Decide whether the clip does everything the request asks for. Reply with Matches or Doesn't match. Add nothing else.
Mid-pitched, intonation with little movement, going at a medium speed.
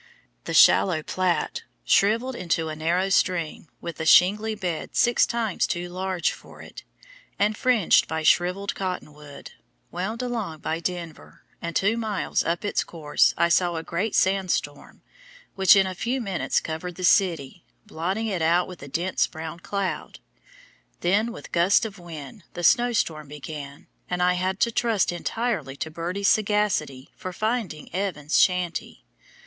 Doesn't match